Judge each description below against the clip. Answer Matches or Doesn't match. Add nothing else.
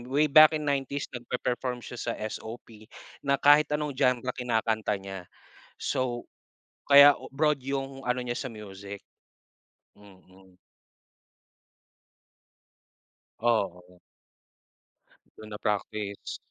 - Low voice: Matches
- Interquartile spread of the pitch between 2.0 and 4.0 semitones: Doesn't match